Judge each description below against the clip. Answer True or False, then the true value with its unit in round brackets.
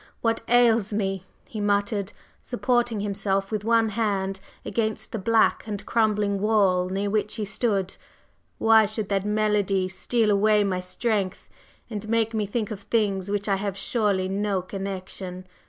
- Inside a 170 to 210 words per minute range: False (155 wpm)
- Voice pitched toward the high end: True (205 Hz)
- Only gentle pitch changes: True (2.0 semitones)